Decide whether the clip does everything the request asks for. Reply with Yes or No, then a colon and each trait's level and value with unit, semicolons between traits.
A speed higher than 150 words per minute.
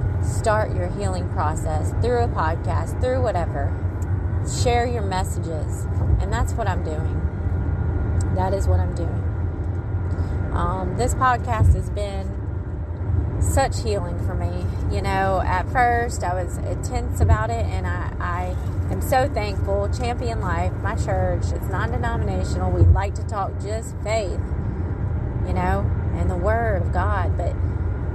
No: average, 145 wpm